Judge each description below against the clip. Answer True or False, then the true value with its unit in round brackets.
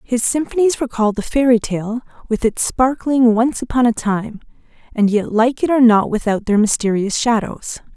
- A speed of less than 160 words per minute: False (175 wpm)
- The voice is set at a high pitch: True (235 Hz)